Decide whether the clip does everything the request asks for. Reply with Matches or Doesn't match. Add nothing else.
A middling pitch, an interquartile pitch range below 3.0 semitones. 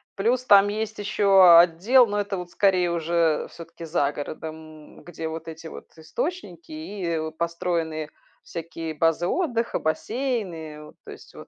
Doesn't match